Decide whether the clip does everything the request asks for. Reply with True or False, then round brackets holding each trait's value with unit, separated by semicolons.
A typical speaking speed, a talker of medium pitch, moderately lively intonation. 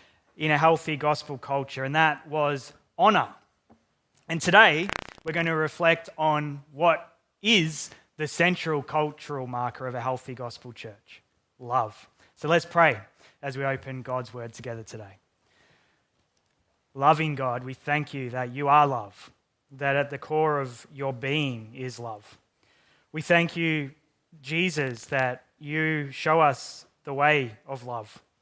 True (145 wpm; 145 Hz; 3.5 semitones)